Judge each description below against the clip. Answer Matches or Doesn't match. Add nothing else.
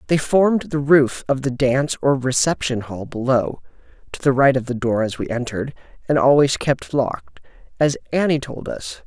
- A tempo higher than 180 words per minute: Doesn't match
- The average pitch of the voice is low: Matches